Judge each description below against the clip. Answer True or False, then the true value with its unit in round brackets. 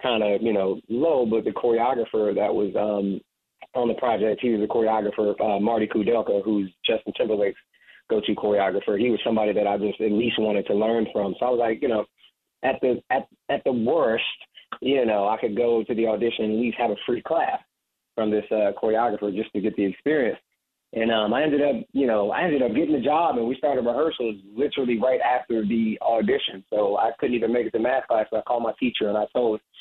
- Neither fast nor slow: False (225 wpm)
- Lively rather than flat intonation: False (2.4 semitones)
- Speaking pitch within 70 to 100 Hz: False (110 Hz)